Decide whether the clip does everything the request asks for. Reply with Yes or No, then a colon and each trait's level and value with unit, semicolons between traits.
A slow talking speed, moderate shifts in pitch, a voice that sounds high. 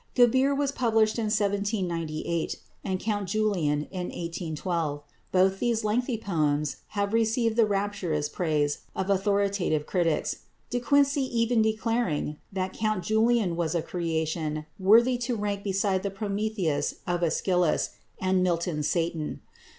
Yes: slow, 130 wpm; average, 4.6 semitones; high, 195 Hz